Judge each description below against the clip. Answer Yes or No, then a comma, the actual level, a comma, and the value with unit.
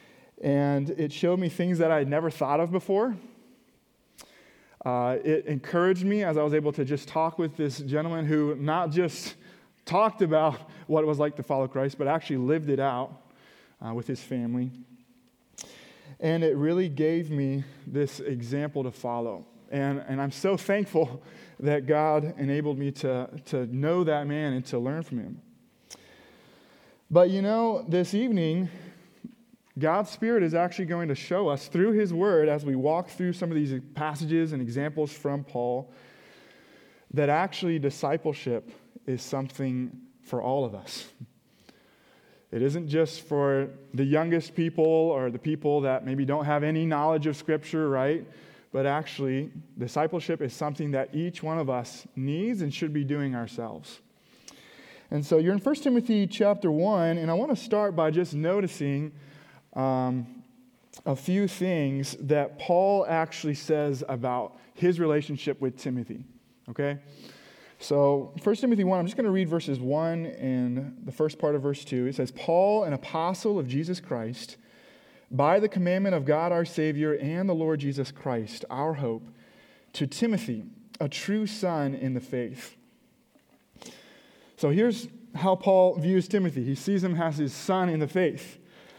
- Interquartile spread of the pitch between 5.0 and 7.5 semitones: No, average, 4.4 semitones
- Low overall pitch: No, medium, 150 Hz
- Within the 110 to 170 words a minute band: Yes, average, 160 wpm